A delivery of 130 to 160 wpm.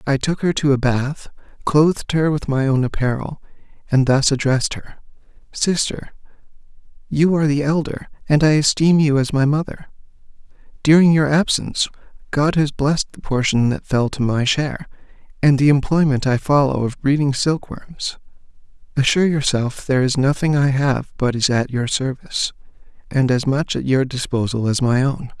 No: average, 170 wpm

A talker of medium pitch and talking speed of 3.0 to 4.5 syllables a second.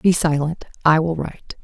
No: medium, 160 Hz; 5.1 syllables/s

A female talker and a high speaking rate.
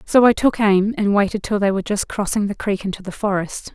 Yes: female; fast, 255 wpm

